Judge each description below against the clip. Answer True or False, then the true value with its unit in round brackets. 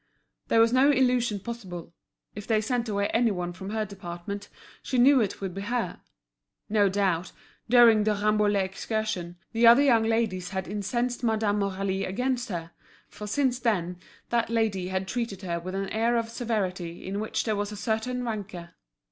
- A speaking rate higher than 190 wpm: False (175 wpm)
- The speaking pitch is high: True (210 Hz)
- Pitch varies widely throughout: False (3.5 semitones)